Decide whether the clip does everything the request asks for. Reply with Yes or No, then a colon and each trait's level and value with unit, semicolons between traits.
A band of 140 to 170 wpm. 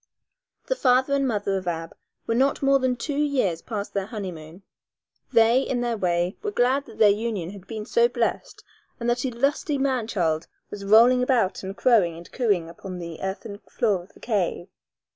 No: average, 190 wpm